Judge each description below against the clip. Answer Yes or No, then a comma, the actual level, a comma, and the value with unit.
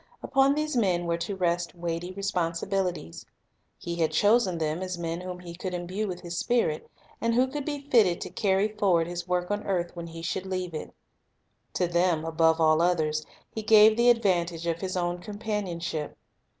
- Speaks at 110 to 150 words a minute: No, average, 185 wpm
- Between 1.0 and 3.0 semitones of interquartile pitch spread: No, average, 3.4 semitones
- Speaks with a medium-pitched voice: Yes, medium, 180 Hz